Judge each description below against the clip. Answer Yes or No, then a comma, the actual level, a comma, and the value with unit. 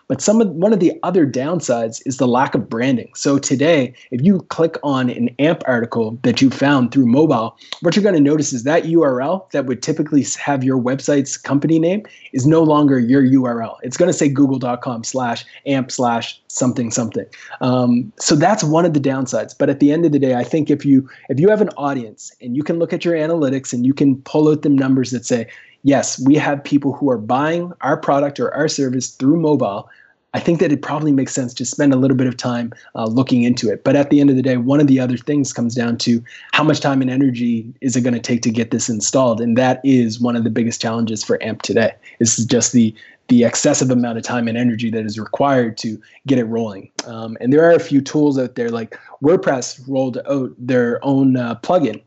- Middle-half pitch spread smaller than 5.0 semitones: Yes, average, 3.3 semitones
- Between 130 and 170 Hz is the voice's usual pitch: Yes, low, 135 Hz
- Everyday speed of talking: No, fast, 235 wpm